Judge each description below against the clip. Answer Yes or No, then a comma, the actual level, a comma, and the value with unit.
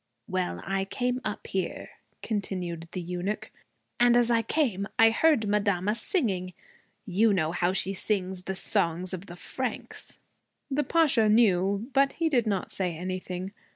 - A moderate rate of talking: Yes, average, 155 wpm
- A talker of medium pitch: No, high, 200 Hz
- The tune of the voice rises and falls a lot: No, average, 4.0 semitones